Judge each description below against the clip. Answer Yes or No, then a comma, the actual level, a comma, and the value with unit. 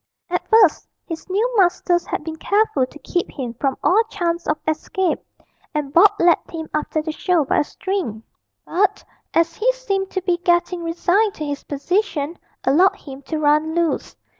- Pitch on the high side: Yes, very high, 340 Hz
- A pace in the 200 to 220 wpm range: No, average, 175 wpm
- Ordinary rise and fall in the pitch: Yes, average, 3.9 semitones